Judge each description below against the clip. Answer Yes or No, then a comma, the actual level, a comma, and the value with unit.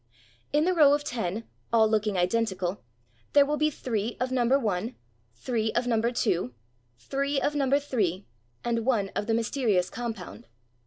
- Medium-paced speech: Yes, average, 160 wpm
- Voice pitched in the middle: No, high, 230 Hz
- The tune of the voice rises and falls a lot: No, average, 4.8 semitones